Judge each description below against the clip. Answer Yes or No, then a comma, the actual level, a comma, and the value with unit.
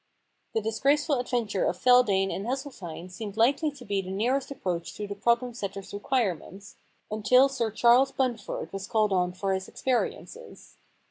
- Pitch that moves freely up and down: No, average, 4.5 semitones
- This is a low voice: No, high, 220 Hz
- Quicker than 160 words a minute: No, average, 155 wpm